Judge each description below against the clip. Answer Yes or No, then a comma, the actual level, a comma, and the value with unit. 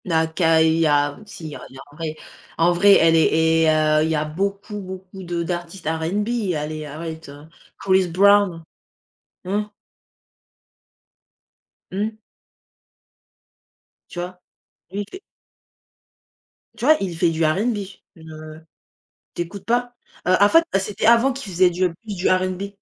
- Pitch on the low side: No, medium, 175 Hz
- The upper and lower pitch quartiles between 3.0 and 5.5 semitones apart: Yes, average, 3.8 semitones